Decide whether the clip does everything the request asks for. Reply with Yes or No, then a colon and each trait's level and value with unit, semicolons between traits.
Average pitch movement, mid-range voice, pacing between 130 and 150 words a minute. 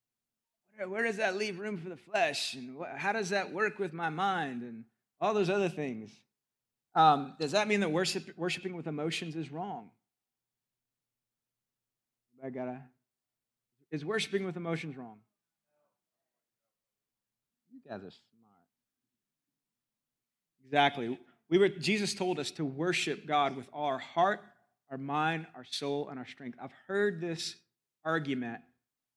No: wide, 6.9 semitones; medium, 150 Hz; average, 140 wpm